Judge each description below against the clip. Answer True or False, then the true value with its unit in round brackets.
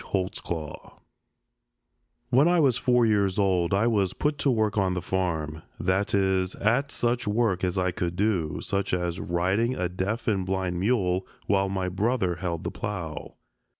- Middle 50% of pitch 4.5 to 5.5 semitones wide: False (3.5 semitones)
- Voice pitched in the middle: False (95 Hz)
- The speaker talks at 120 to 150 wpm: False (165 wpm)